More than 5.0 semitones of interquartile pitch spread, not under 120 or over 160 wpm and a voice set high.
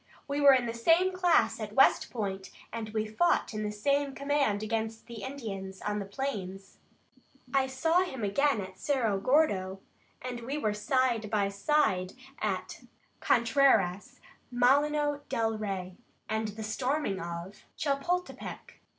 Yes: wide, 5.4 semitones; average, 140 wpm; high, 230 Hz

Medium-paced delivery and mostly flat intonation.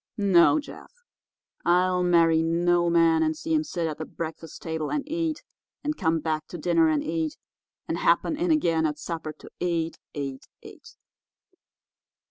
Yes: average, 160 wpm; narrow, 2.2 semitones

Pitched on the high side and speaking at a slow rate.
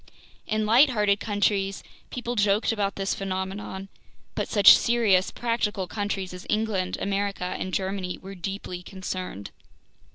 Yes: high, 195 Hz; slow, 125 wpm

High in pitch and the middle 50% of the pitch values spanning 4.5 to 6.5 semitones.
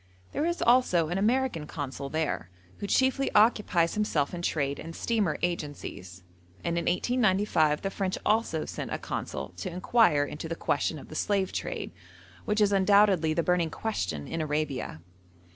No: medium, 175 Hz; wide, 5.6 semitones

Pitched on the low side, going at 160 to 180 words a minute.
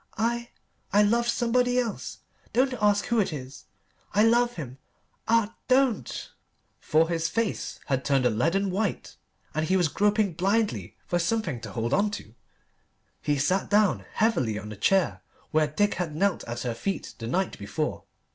No: high, 190 Hz; average, 165 wpm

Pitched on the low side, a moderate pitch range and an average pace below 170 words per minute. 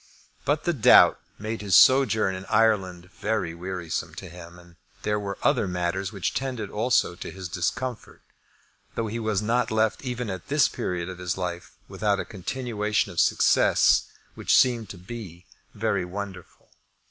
Yes: low, 100 Hz; average, 3.8 semitones; average, 160 wpm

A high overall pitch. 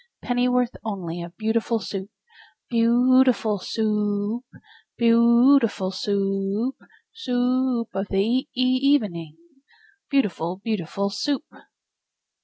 Yes: high, 225 Hz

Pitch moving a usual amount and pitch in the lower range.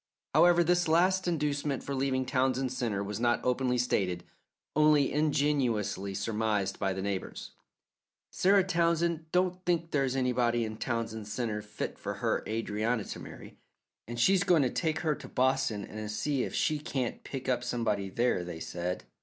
No: wide, 6.0 semitones; low, 125 Hz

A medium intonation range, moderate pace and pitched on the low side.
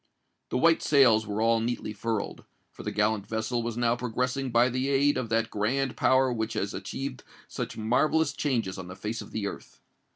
Yes: average, 3.1 semitones; average, 195 wpm; low, 115 Hz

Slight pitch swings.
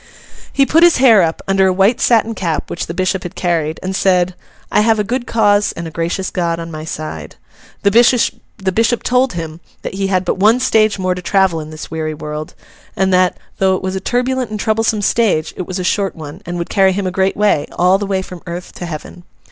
No: average, 3.8 semitones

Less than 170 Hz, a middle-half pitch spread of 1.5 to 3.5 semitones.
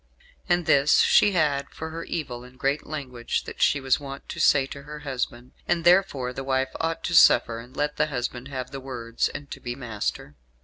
Yes: low, 135 Hz; average, 3.1 semitones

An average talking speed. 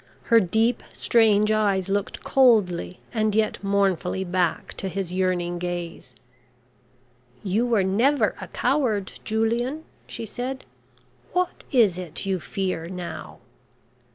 No: slow, 120 wpm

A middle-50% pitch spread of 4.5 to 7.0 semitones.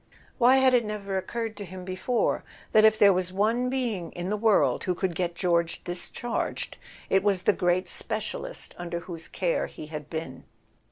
No: average, 3.7 semitones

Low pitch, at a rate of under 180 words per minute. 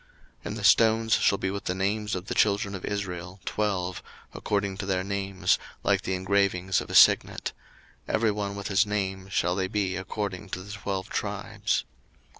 No: low, 100 Hz; average, 185 wpm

